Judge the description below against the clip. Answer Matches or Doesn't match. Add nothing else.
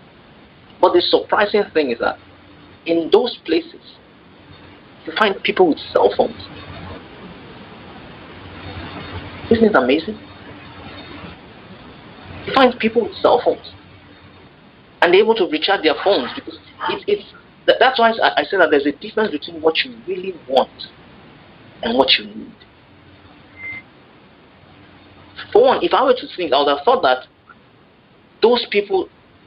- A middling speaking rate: Doesn't match